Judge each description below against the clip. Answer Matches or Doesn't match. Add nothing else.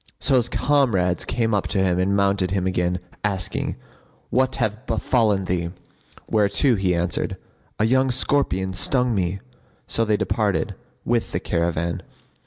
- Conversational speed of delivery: Matches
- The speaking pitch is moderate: Doesn't match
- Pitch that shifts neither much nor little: Matches